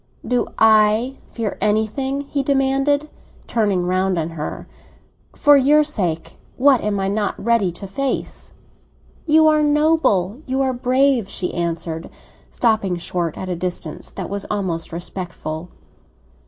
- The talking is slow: Yes, slow, 130 wpm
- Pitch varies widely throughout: Yes, wide, 7.0 semitones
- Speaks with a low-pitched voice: No, high, 215 Hz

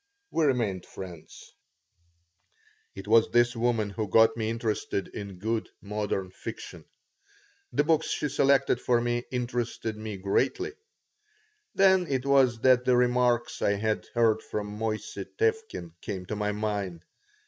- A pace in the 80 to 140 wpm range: Yes, slow, 135 wpm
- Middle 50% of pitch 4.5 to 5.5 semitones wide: No, average, 3.2 semitones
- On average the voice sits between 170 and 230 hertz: No, low, 115 Hz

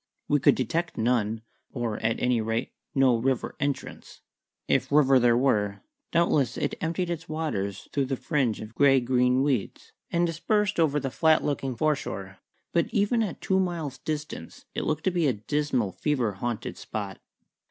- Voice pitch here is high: No, low, 135 Hz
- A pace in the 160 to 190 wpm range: Yes, average, 165 wpm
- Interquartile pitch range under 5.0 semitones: No, average, 5.3 semitones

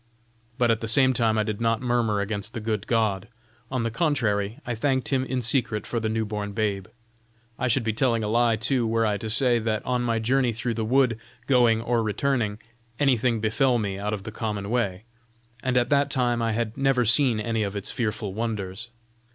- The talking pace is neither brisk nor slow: No, fast, 210 wpm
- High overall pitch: No, low, 115 Hz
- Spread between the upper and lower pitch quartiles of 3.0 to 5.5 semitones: No, narrow, 2.5 semitones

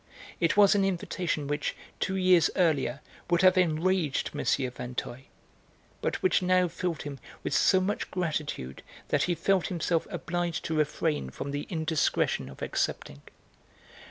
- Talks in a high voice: No, medium, 165 Hz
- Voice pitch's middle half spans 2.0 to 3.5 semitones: No, average, 4.0 semitones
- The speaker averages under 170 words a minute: Yes, average, 145 wpm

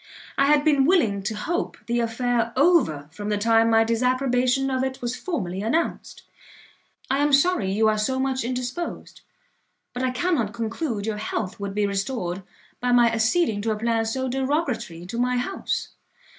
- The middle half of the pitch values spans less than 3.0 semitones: No, average, 3.7 semitones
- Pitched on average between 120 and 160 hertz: No, high, 240 Hz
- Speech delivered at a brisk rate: No, average, 170 wpm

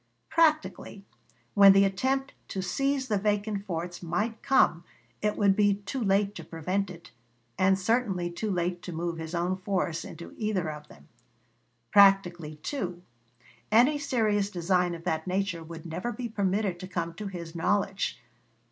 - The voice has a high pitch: Yes, high, 195 Hz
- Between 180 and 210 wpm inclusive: No, average, 155 wpm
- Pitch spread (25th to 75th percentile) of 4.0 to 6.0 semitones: No, average, 3.3 semitones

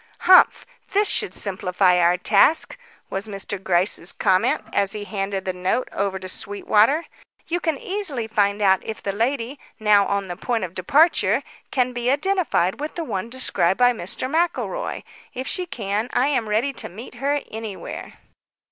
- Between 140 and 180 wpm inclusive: Yes, average, 165 wpm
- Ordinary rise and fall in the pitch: No, wide, 6.0 semitones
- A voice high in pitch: Yes, high, 220 Hz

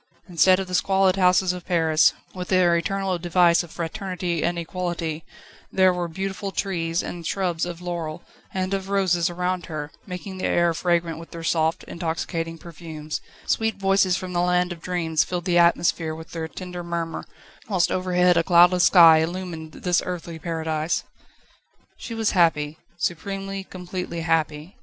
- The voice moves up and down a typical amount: No, narrow, 1.9 semitones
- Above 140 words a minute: Yes, average, 160 wpm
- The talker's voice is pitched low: No, medium, 175 Hz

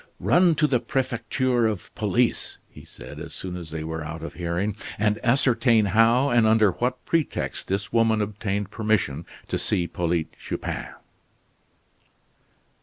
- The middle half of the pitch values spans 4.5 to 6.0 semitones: Yes, wide, 5.5 semitones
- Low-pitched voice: Yes, low, 105 Hz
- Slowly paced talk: No, average, 145 wpm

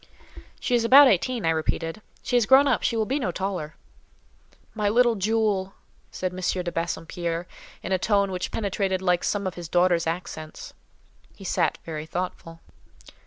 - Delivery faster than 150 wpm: Yes, average, 165 wpm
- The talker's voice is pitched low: No, medium, 185 Hz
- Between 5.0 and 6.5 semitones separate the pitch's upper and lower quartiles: No, average, 4.3 semitones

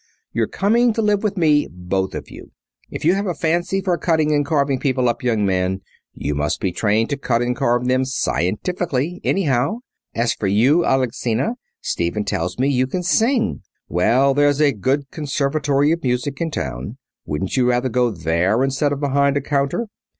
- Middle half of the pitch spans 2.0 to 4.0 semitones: No, average, 5.3 semitones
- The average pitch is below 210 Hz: Yes, low, 135 Hz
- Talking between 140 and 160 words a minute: No, average, 185 wpm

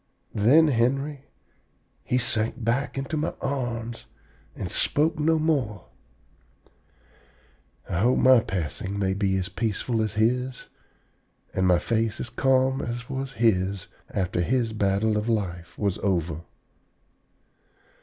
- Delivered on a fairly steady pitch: No, average, 4.9 semitones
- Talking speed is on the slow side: Yes, slow, 125 wpm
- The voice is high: No, low, 115 Hz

